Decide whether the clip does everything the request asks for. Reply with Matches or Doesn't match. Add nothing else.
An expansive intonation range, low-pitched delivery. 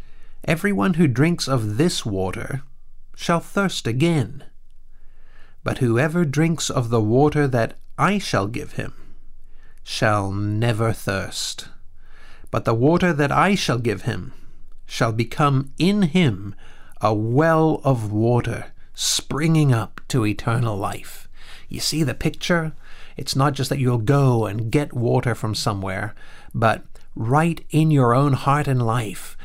Matches